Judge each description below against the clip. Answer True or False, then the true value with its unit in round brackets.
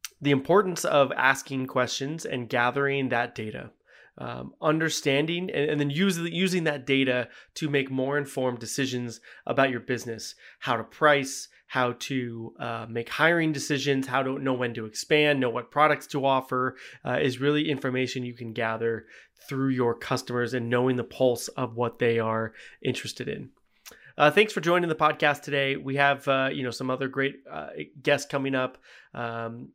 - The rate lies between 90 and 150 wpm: False (170 wpm)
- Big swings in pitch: False (2.8 semitones)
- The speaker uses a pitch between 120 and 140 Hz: True (135 Hz)